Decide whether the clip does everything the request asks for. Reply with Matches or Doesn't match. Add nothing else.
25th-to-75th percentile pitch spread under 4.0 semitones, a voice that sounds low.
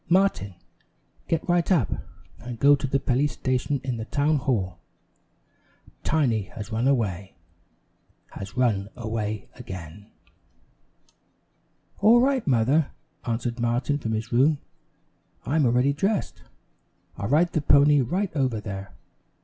Doesn't match